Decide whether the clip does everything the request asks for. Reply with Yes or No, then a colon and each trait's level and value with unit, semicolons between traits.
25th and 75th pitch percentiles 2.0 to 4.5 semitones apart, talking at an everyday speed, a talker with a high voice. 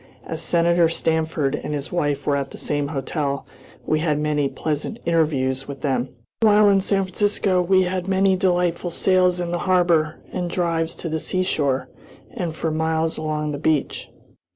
No: average, 3.4 semitones; average, 170 wpm; medium, 165 Hz